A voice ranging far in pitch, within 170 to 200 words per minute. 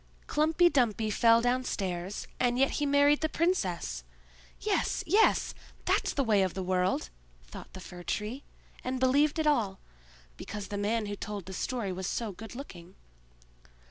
No: wide, 6.5 semitones; average, 160 wpm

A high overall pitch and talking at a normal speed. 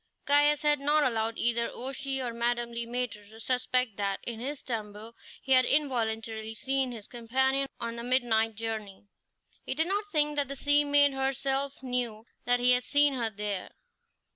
Yes: very high, 250 Hz; average, 175 wpm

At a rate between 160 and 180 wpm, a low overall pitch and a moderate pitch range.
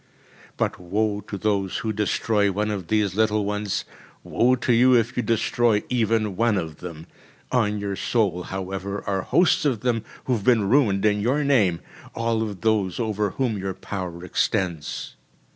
Yes: average, 170 wpm; low, 105 Hz; average, 3.0 semitones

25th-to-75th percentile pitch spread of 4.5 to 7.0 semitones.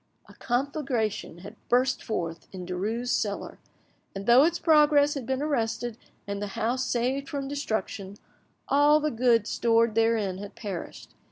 Yes: average, 5.1 semitones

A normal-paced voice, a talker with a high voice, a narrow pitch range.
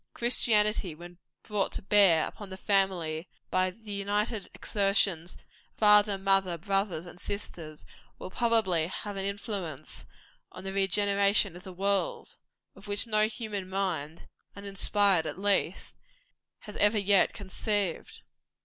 No: slow, 130 wpm; high, 195 Hz; narrow, 2.1 semitones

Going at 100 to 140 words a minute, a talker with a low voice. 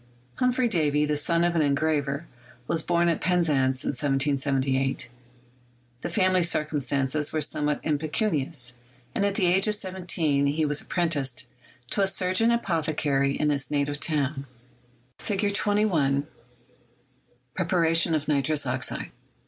No: slow, 135 wpm; medium, 155 Hz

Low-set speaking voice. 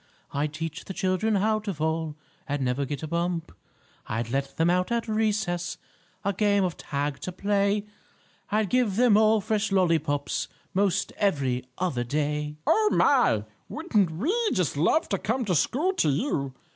No: medium, 180 Hz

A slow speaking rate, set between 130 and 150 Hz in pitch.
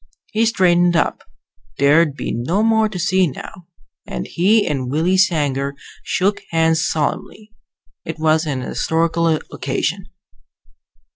No: slow, 125 wpm; medium, 165 Hz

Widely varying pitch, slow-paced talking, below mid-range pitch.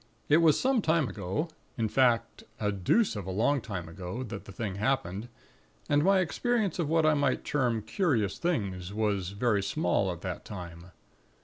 No: wide, 7.4 semitones; average, 180 wpm; low, 115 Hz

